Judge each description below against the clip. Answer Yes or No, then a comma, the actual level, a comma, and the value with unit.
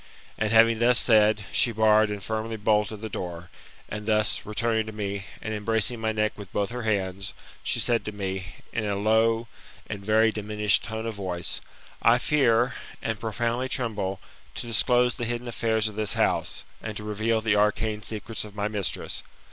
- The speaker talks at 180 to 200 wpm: Yes, average, 185 wpm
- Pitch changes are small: Yes, narrow, 1.6 semitones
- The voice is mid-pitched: No, low, 110 Hz